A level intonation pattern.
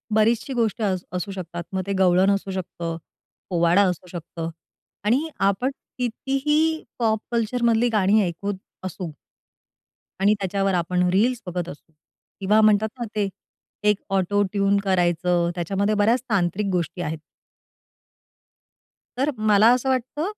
No: average, 3.8 semitones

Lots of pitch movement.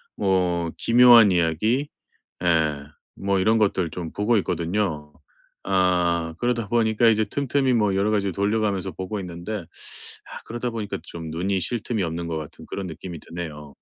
No: average, 4.3 semitones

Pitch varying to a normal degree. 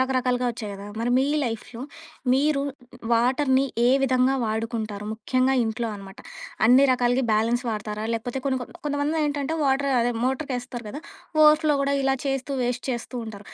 Yes: average, 3.0 semitones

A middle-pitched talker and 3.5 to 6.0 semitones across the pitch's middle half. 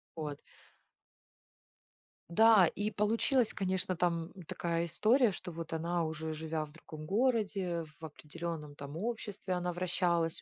Yes: medium, 175 Hz; average, 3.8 semitones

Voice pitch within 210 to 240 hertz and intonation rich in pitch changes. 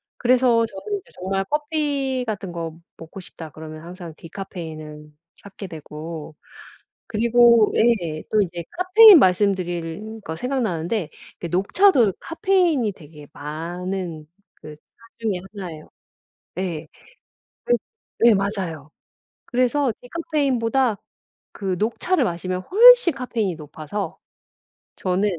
No: high, 195 Hz; wide, 6.9 semitones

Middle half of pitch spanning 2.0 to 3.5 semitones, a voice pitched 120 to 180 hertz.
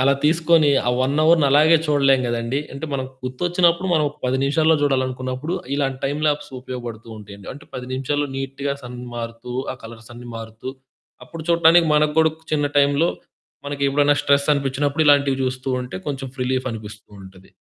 Yes: average, 2.8 semitones; medium, 140 Hz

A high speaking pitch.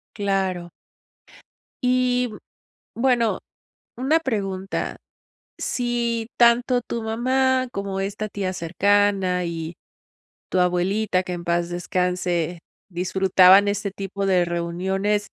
Yes: high, 195 Hz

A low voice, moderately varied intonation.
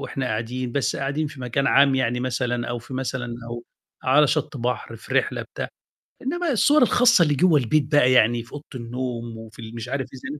Yes: low, 130 Hz; average, 3.4 semitones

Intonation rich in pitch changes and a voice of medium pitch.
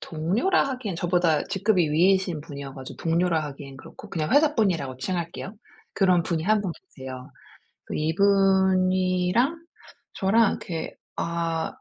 No: average, 3.5 semitones; medium, 180 Hz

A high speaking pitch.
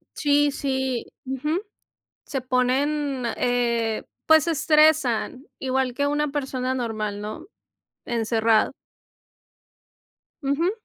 Yes: very high, 265 Hz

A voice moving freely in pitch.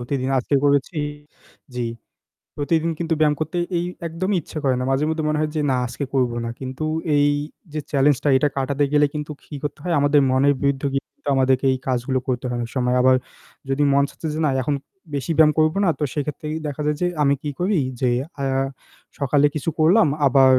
No: average, 2.8 semitones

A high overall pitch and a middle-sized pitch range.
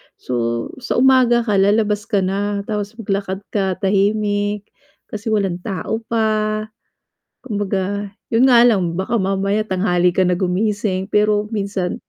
No: high, 205 Hz; narrow, 2.1 semitones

